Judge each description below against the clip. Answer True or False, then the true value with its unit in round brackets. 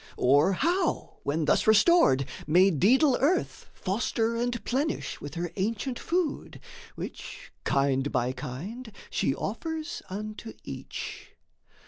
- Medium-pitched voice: False (210 Hz)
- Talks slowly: True (115 wpm)